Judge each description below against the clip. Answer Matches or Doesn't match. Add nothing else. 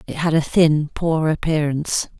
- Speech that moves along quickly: Doesn't match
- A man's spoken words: Doesn't match